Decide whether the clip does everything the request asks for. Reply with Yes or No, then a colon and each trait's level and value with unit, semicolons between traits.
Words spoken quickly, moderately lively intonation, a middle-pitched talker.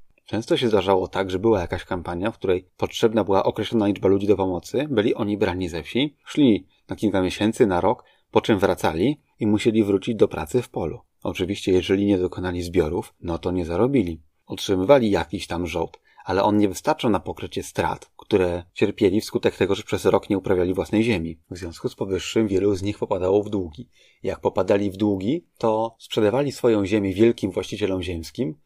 No: fast, 190 wpm; average, 3.0 semitones; low, 100 Hz